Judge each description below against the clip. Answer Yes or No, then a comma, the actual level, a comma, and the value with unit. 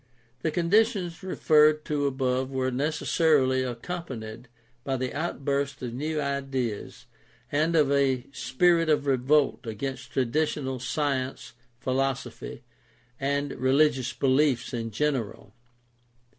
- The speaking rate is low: Yes, slow, 115 wpm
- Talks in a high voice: No, low, 135 Hz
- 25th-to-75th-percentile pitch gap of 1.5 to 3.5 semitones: Yes, average, 2.8 semitones